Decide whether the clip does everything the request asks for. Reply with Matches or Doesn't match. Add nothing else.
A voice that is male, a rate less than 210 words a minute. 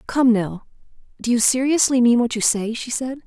Doesn't match